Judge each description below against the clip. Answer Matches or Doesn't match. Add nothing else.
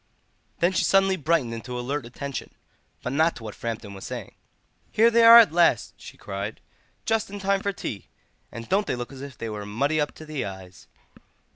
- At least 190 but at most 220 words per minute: Matches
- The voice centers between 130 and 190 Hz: Matches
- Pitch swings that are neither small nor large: Doesn't match